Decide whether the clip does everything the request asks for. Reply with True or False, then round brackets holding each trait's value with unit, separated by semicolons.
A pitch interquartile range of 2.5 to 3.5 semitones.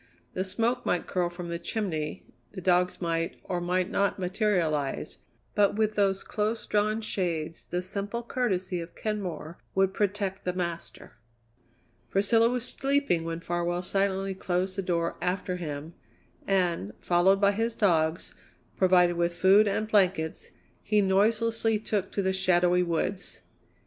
True (2.9 semitones)